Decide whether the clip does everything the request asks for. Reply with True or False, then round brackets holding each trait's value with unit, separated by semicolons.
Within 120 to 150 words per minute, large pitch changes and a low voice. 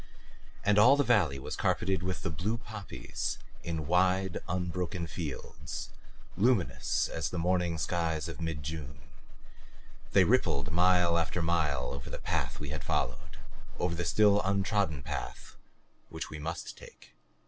False (145 wpm; 3.4 semitones; 85 Hz)